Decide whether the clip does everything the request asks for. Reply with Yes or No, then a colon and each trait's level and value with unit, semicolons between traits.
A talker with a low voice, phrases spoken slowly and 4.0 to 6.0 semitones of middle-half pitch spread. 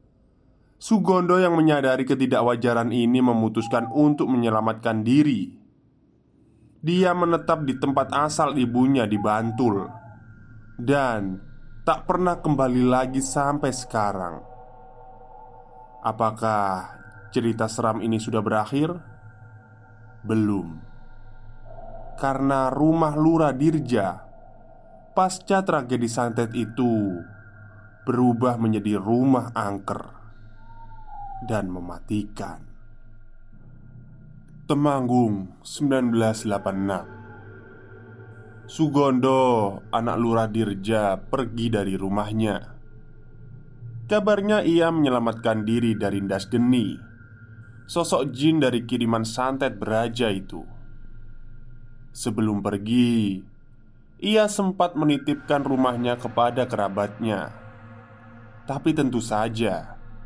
No: low, 120 Hz; slow, 80 wpm; average, 3.5 semitones